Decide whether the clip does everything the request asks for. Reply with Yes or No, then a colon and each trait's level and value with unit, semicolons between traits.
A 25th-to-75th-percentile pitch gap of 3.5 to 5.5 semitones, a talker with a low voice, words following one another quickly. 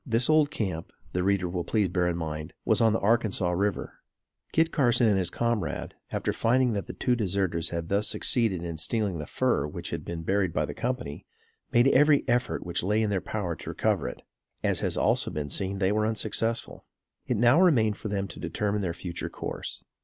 Yes: average, 4.8 semitones; low, 100 Hz; fast, 210 wpm